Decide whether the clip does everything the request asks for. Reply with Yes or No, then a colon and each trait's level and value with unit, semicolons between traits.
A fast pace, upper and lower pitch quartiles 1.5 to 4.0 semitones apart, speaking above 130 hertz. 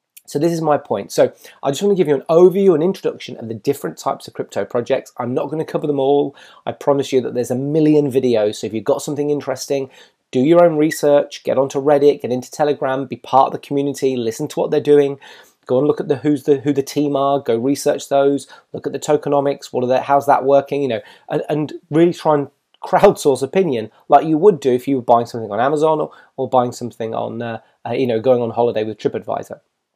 Yes: fast, 245 wpm; narrow, 2.6 semitones; medium, 140 Hz